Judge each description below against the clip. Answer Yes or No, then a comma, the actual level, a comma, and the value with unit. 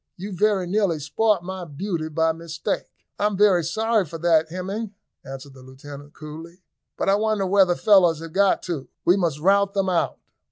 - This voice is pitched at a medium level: Yes, medium, 175 Hz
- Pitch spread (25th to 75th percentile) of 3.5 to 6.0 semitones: Yes, average, 3.8 semitones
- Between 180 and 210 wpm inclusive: Yes, average, 190 wpm